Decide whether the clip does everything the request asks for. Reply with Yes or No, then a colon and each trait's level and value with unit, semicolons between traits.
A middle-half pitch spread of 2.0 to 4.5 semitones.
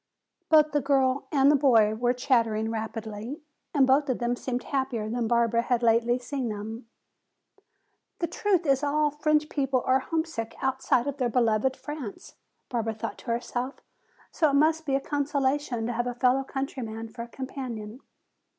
Yes: average, 3.4 semitones